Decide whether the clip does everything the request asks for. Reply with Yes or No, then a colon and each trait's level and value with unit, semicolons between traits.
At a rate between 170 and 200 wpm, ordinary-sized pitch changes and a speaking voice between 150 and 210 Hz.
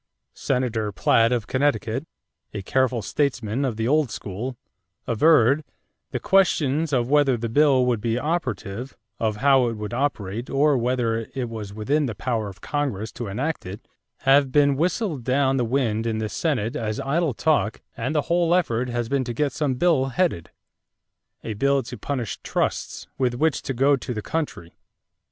No: average, 175 wpm; average, 4.1 semitones; low, 130 Hz